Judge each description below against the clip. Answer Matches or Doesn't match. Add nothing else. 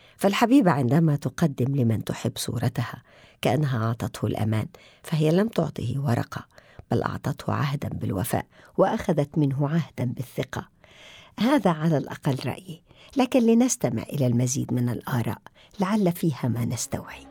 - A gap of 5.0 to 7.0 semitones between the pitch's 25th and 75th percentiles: Matches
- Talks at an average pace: Matches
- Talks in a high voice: Doesn't match